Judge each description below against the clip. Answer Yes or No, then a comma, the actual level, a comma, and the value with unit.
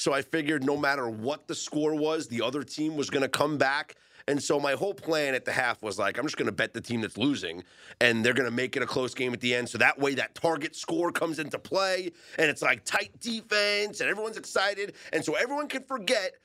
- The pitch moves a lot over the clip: Yes, wide, 7.0 semitones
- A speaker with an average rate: No, fast, 245 wpm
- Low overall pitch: No, medium, 150 Hz